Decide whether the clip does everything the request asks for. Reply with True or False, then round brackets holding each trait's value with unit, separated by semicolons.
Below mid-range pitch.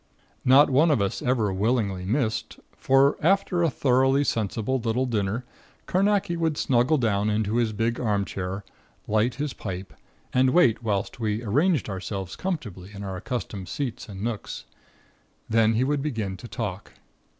True (115 Hz)